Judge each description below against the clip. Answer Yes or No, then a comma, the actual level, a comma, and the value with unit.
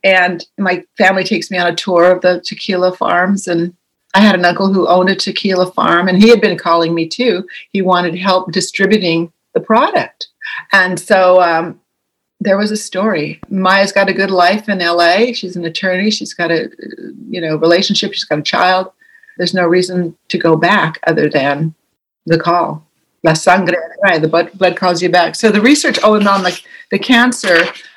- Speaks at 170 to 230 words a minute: Yes, average, 185 wpm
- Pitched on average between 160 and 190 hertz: Yes, medium, 185 Hz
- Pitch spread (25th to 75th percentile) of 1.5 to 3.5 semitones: Yes, narrow, 2.6 semitones